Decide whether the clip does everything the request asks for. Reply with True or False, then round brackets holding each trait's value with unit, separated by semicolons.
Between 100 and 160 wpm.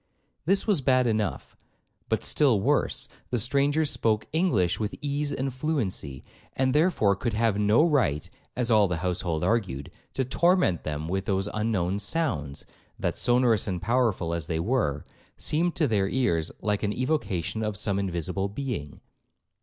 True (155 wpm)